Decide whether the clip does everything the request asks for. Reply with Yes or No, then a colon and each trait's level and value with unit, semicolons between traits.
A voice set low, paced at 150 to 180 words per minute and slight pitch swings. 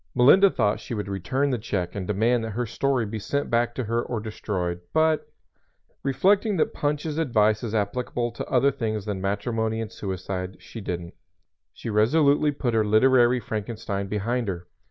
No: low, 115 Hz; average, 175 wpm; average, 4.0 semitones